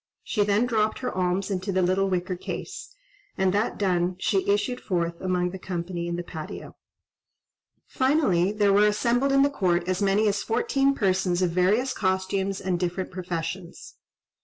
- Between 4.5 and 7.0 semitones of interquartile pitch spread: No, average, 2.8 semitones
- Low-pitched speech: No, high, 190 Hz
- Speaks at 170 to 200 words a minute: No, average, 160 wpm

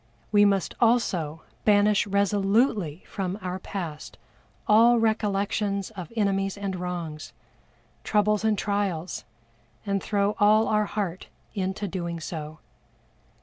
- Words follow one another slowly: Yes, slow, 110 wpm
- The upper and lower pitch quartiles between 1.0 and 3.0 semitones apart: Yes, narrow, 2.6 semitones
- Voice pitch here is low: No, high, 200 Hz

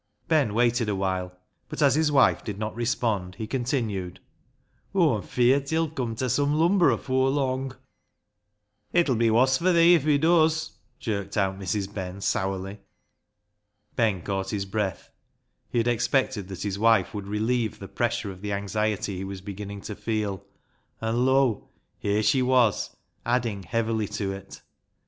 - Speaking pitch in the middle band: No, low, 110 Hz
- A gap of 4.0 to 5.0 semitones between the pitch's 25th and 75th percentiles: Yes, average, 4.7 semitones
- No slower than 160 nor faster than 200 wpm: Yes, average, 170 wpm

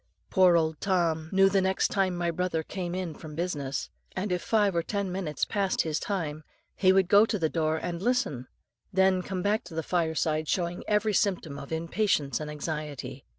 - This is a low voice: No, medium, 175 Hz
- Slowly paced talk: No, average, 190 wpm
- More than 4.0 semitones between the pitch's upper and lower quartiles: No, average, 3.4 semitones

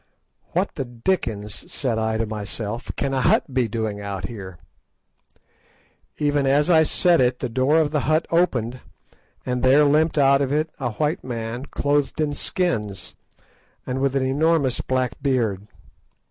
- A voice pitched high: No, low, 130 Hz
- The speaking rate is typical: Yes, average, 155 wpm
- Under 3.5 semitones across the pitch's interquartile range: No, average, 4.3 semitones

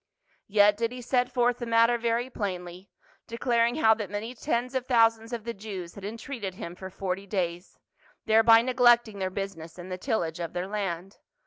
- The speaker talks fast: No, average, 190 wpm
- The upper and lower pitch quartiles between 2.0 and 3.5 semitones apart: No, average, 3.9 semitones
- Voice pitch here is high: Yes, high, 220 Hz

